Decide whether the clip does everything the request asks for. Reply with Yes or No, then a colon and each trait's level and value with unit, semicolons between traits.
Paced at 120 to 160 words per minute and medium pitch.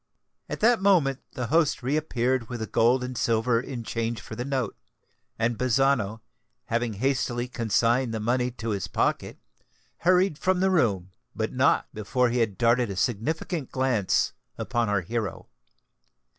No: average, 155 wpm; low, 120 Hz